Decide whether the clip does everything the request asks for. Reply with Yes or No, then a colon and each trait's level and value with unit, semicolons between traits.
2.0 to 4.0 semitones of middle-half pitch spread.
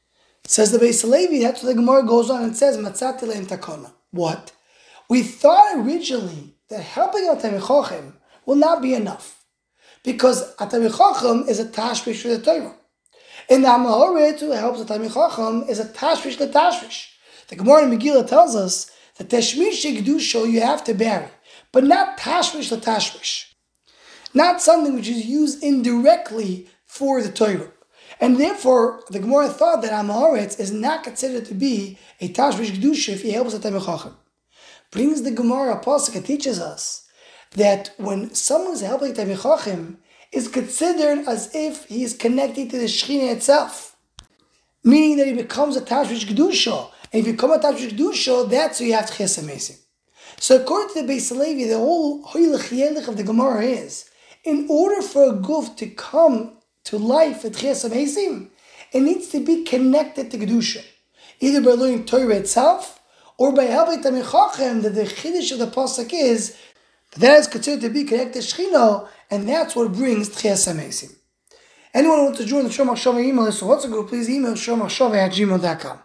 No: average, 4.7 semitones